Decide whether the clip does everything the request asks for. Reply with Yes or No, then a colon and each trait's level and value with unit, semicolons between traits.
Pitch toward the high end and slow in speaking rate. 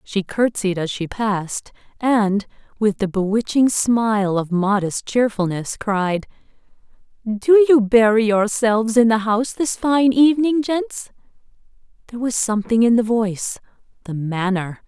Yes: high, 220 Hz; slow, 130 wpm